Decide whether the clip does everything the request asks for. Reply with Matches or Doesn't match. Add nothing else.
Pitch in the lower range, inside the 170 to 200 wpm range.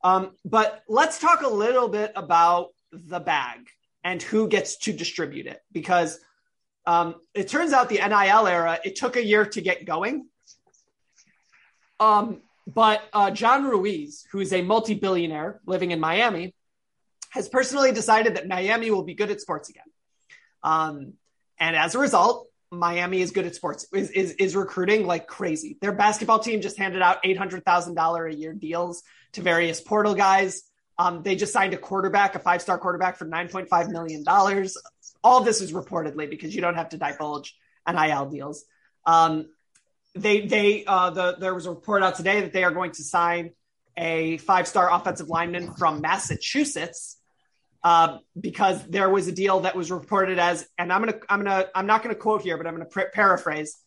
Doesn't match